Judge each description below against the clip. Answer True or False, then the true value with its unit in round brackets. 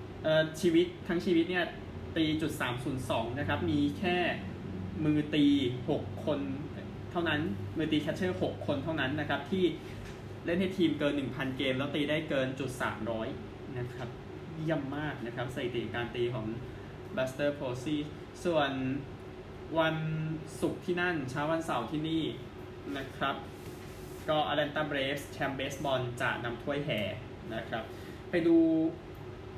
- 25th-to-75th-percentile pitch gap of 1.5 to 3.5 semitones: False (4.2 semitones)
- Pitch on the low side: False (145 Hz)